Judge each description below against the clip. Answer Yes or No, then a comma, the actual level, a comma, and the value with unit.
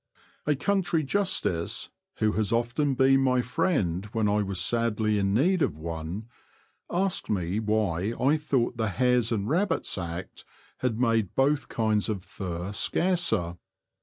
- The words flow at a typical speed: Yes, average, 145 wpm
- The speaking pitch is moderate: No, low, 110 Hz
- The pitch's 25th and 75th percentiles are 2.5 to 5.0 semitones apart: No, wide, 5.5 semitones